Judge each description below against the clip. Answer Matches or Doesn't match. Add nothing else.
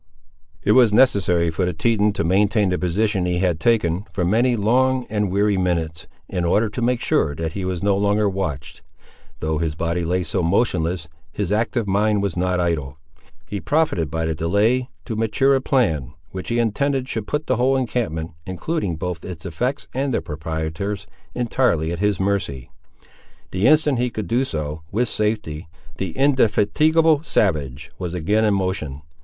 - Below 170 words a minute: Doesn't match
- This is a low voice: Matches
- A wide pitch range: Matches